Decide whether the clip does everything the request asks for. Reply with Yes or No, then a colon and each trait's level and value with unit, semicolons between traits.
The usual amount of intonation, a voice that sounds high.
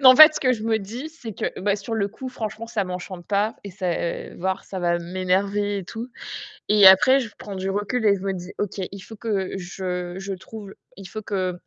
Yes: average, 3.0 semitones; high, 200 Hz